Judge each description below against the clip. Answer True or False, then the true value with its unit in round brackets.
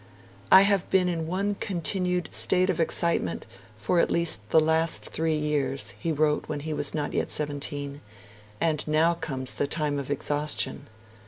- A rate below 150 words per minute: False (165 wpm)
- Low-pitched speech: False (155 Hz)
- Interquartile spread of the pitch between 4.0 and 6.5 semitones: False (2.8 semitones)